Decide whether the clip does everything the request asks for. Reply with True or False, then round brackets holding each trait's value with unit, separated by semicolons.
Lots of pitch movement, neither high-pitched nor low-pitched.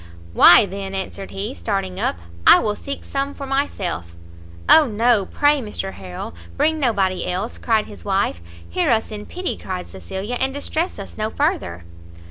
False (6.1 semitones; 210 Hz)